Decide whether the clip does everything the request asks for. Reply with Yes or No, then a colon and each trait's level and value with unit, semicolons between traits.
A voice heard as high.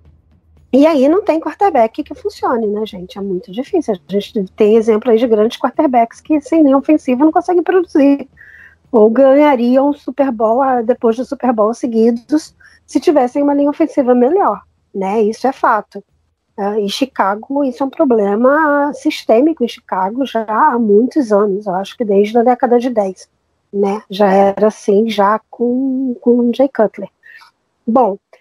Yes: high, 245 Hz